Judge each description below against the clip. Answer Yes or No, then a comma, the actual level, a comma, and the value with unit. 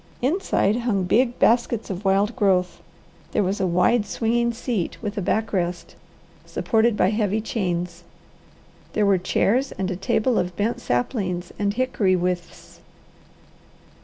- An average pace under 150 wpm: Yes, average, 140 wpm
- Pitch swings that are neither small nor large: Yes, average, 4.0 semitones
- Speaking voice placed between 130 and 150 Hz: No, high, 205 Hz